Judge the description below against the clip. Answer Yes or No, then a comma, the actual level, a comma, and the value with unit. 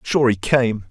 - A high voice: No, low, 120 Hz